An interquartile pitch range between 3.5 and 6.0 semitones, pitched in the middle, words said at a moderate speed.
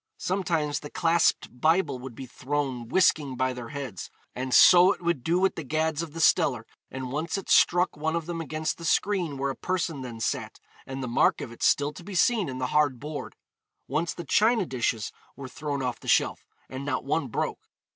No: average, 4.5 semitones; medium, 150 Hz; fast, 210 wpm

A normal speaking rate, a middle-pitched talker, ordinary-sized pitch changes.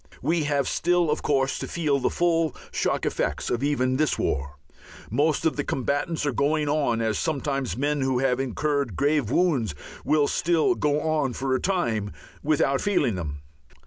Yes: average, 175 wpm; medium, 145 Hz; average, 3.2 semitones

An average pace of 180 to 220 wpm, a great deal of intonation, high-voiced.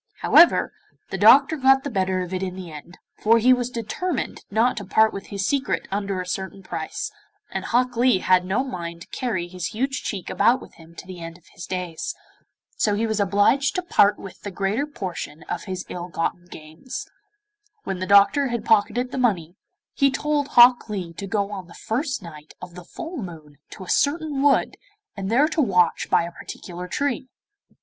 Yes: average, 200 wpm; wide, 5.8 semitones; high, 200 Hz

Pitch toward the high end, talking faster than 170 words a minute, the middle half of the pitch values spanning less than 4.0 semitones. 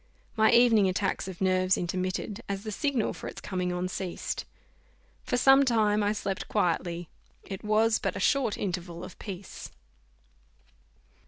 No: high, 195 Hz; average, 150 wpm; average, 3.1 semitones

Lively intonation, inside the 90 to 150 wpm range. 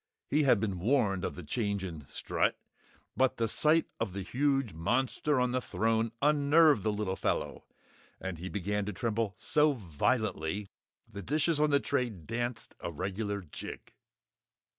No: wide, 5.9 semitones; average, 160 wpm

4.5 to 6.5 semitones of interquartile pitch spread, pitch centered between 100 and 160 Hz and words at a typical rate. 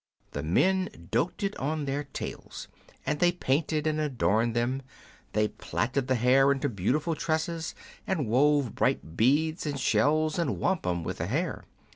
Yes: average, 4.8 semitones; medium, 140 Hz; average, 150 wpm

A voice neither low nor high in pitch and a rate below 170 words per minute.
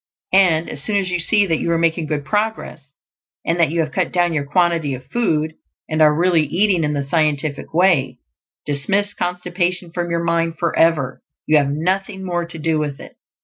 No: medium, 165 Hz; average, 195 wpm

